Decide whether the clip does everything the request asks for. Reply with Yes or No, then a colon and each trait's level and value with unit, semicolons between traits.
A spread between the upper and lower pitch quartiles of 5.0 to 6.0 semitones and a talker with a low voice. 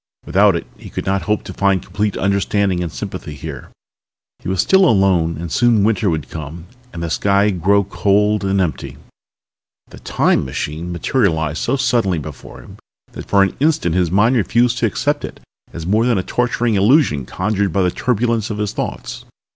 No: average, 4.2 semitones; low, 100 Hz